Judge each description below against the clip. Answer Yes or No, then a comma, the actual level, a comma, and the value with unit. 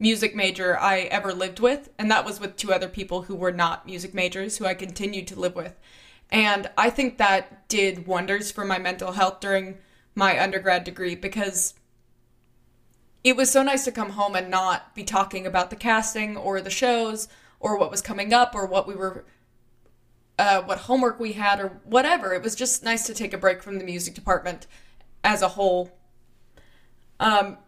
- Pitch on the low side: No, high, 195 Hz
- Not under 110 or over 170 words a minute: No, average, 190 wpm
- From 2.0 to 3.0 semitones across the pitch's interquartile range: Yes, narrow, 2.5 semitones